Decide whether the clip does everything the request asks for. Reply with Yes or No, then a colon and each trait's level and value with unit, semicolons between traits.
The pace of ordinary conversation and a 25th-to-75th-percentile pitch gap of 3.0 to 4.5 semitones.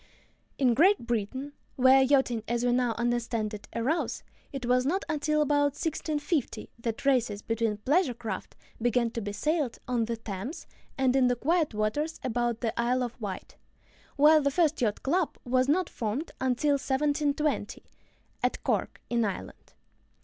Yes: average, 155 wpm; average, 3.9 semitones